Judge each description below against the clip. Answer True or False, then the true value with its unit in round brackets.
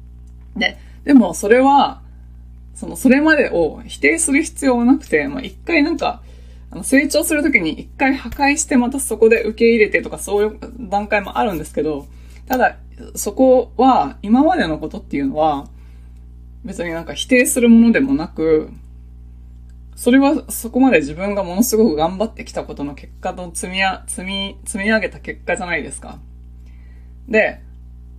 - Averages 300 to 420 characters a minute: True (315 characters per minute)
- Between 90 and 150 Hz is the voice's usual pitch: False (200 Hz)